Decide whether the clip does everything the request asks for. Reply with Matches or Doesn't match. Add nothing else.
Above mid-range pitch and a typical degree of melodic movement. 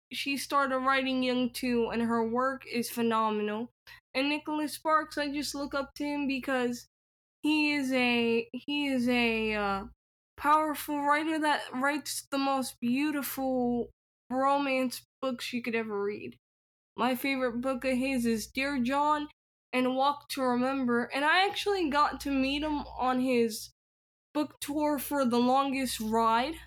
Matches